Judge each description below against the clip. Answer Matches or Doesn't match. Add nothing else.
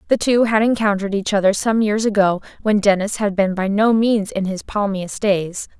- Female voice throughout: Matches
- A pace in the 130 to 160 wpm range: Doesn't match